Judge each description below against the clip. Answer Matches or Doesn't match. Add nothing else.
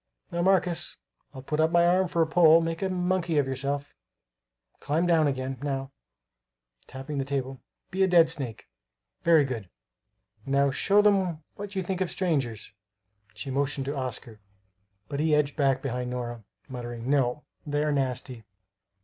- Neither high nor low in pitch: Matches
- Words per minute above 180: Doesn't match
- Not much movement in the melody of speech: Doesn't match